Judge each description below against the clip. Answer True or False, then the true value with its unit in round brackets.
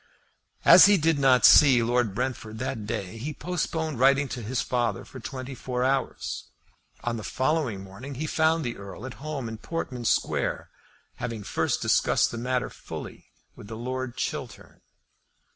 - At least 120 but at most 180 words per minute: True (160 wpm)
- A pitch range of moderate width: True (3.3 semitones)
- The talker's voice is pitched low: True (125 Hz)